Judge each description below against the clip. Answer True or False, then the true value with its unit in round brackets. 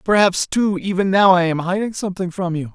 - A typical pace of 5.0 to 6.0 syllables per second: True (5.7 syllables/s)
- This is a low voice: False (185 Hz)